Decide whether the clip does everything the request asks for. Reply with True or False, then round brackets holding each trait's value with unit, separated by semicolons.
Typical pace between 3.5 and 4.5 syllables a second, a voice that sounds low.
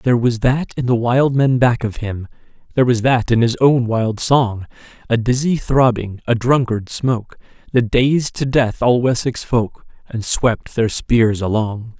True (4.3 syllables/s; 120 Hz)